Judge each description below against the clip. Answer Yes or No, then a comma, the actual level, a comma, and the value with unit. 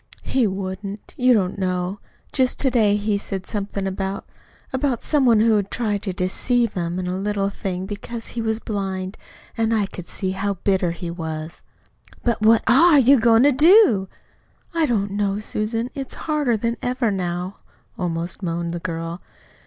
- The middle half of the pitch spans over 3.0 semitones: Yes, average, 3.8 semitones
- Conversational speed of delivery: Yes, average, 175 wpm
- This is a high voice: Yes, high, 205 Hz